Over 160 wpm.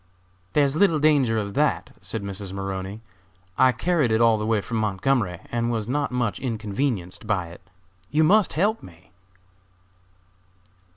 No: average, 155 wpm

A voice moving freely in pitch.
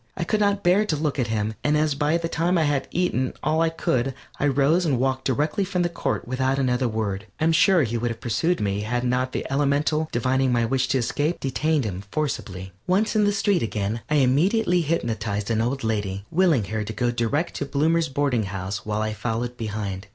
Yes: wide, 6.0 semitones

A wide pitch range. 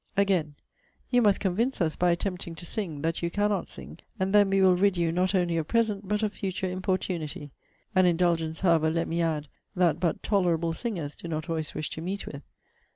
No: average, 3.0 semitones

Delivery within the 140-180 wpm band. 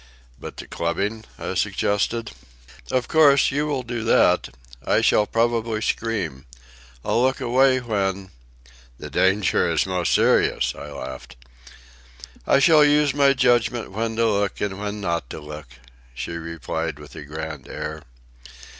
Yes: average, 145 wpm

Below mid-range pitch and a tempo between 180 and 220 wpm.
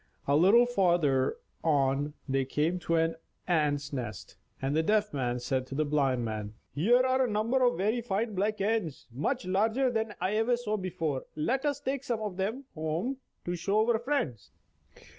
No: medium, 185 Hz; average, 185 wpm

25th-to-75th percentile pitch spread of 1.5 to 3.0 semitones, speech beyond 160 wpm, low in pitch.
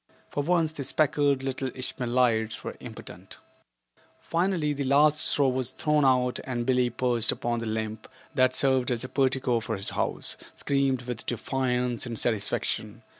No: narrow, 2.6 semitones; average, 155 wpm; low, 130 Hz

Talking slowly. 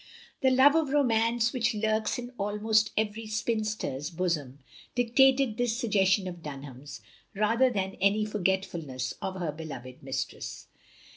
Yes: slow, 130 wpm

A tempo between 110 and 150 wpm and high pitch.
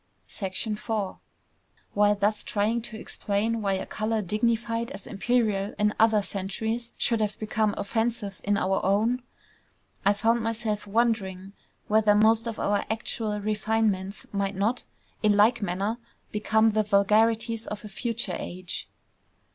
Yes: slow, 135 wpm; high, 215 Hz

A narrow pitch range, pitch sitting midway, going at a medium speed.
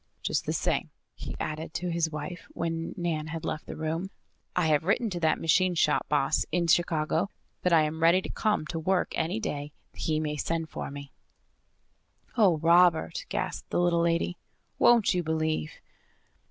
Yes: narrow, 2.2 semitones; medium, 165 Hz; average, 175 wpm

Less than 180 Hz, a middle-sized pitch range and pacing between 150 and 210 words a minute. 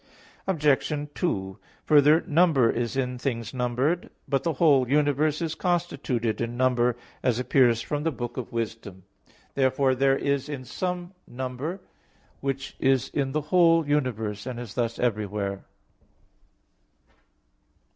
No: low, 135 Hz; average, 3.9 semitones; slow, 135 wpm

